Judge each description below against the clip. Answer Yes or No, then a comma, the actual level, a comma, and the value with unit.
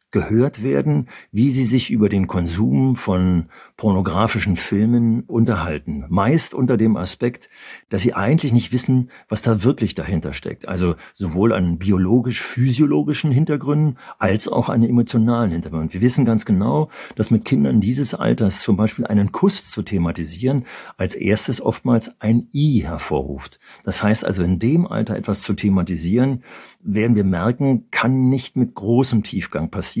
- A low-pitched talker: Yes, low, 115 Hz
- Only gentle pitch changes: No, average, 4.8 semitones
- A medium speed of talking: Yes, average, 150 wpm